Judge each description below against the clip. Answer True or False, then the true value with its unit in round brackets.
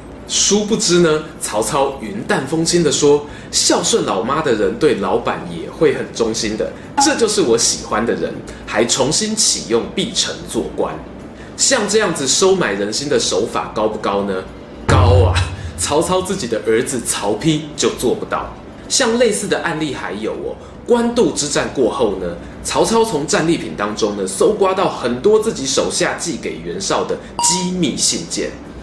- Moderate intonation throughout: False (8.0 semitones)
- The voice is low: False (185 Hz)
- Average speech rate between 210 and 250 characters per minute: True (245 characters per minute)